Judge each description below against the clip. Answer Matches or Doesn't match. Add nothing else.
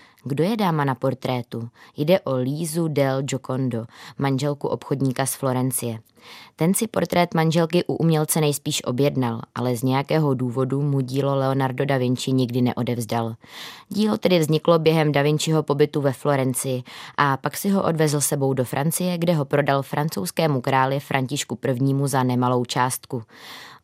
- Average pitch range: Matches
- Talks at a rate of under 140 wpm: Doesn't match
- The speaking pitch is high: Doesn't match